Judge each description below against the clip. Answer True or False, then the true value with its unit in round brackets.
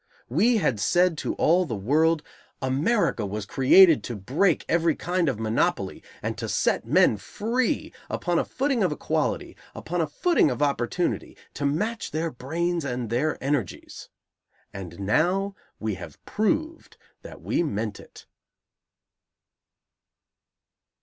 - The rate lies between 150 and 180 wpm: False (135 wpm)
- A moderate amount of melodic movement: False (7.1 semitones)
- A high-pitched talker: False (155 Hz)